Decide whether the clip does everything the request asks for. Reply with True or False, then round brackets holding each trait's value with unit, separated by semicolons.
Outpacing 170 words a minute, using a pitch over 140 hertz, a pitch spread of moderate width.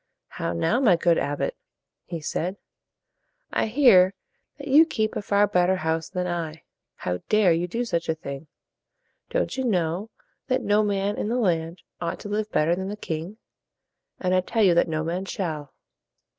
True (180 wpm; 185 Hz; 4.4 semitones)